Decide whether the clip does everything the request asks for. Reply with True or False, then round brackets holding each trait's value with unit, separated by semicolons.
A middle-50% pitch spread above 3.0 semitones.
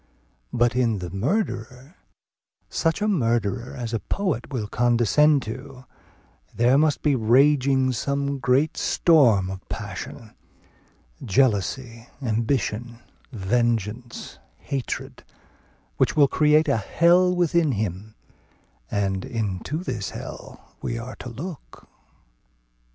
True (4.4 semitones)